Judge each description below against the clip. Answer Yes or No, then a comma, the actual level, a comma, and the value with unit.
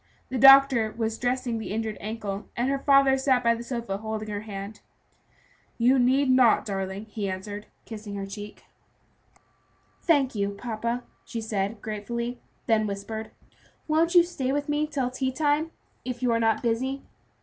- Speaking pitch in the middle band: No, high, 230 Hz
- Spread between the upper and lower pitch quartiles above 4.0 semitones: No, average, 3.7 semitones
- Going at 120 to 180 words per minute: Yes, average, 160 wpm